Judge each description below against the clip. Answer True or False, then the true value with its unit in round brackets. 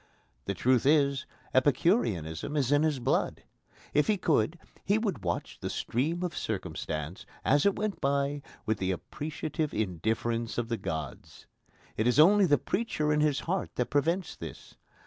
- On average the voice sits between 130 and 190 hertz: True (140 Hz)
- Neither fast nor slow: True (160 wpm)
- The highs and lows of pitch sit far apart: True (6.2 semitones)